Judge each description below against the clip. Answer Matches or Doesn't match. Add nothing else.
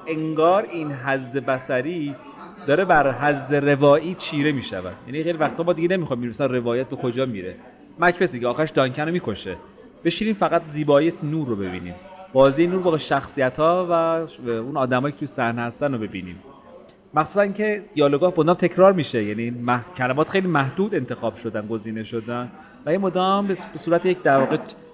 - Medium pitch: Matches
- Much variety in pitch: Matches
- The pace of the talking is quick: Matches